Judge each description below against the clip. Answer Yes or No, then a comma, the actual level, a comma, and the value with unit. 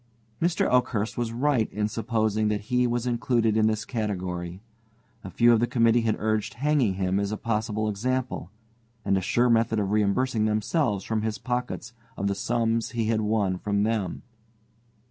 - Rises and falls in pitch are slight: Yes, narrow, 2.3 semitones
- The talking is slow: No, average, 175 wpm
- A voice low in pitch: Yes, low, 110 Hz